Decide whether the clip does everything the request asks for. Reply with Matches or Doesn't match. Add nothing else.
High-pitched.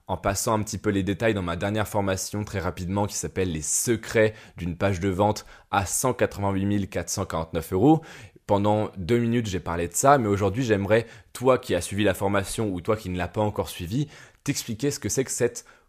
Doesn't match